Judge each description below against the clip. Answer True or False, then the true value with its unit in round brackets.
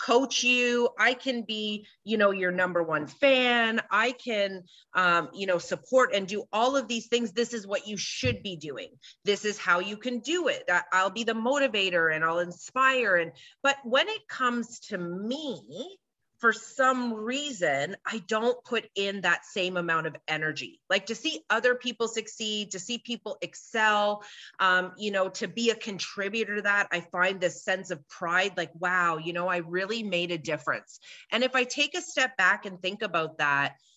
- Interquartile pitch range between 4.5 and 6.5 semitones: True (5.0 semitones)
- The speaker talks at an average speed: True (190 wpm)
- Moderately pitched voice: False (210 Hz)